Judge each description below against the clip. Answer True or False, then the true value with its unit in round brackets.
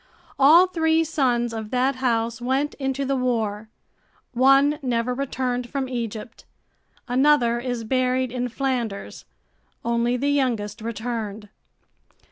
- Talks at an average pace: False (115 wpm)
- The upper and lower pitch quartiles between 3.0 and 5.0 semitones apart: False (2.6 semitones)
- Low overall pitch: False (250 Hz)